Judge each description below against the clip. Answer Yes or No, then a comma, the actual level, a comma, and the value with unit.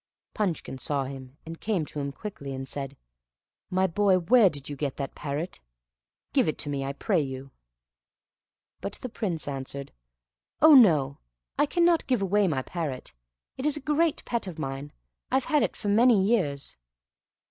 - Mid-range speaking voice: Yes, medium, 165 Hz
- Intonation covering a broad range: Yes, wide, 7.6 semitones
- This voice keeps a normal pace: Yes, average, 170 wpm